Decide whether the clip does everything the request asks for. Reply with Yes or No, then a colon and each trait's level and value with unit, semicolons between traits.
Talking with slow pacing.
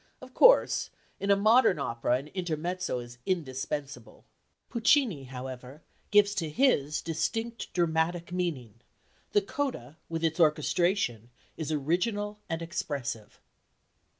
Yes: slow, 115 wpm